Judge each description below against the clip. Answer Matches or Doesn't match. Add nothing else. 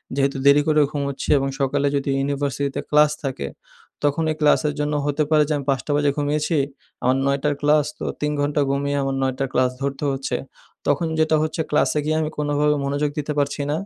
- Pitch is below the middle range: Doesn't match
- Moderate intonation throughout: Doesn't match